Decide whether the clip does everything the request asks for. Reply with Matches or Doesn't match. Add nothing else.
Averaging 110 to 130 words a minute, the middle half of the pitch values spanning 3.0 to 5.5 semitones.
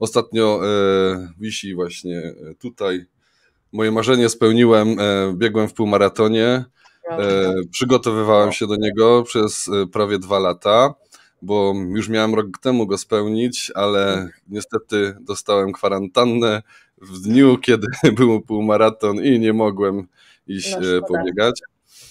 Doesn't match